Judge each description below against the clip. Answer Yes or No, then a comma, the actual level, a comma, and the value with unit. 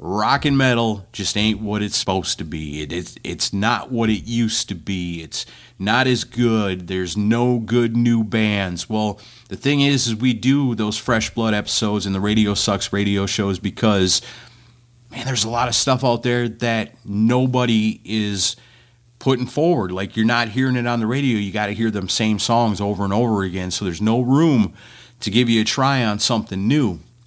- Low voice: Yes, low, 110 Hz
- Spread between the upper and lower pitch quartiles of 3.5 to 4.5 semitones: No, average, 3.0 semitones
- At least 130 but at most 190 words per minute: No, average, 200 wpm